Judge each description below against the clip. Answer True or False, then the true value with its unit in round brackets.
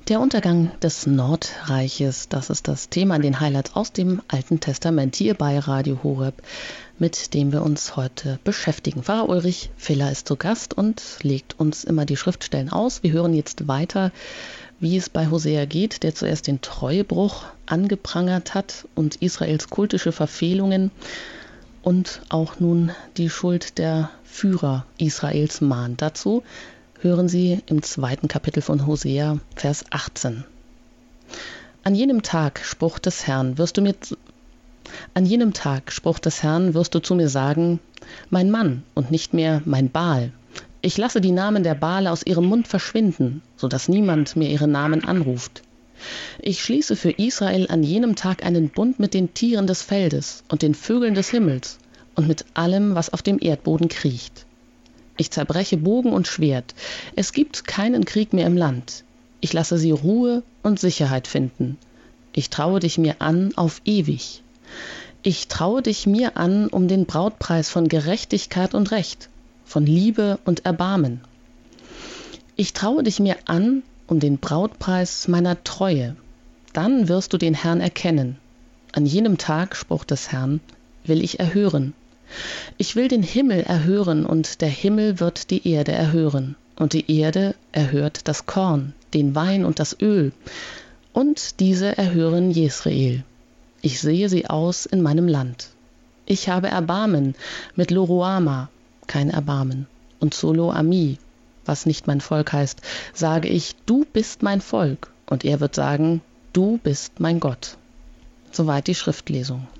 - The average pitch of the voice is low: False (165 Hz)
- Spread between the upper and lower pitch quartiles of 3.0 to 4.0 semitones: False (4.9 semitones)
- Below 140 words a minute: False (155 wpm)